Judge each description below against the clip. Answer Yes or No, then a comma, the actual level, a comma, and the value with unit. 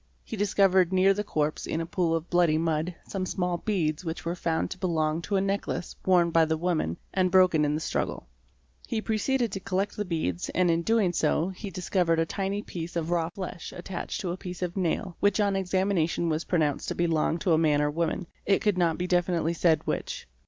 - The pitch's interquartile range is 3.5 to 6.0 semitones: No, average, 2.7 semitones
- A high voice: No, medium, 175 Hz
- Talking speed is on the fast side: Yes, fast, 215 wpm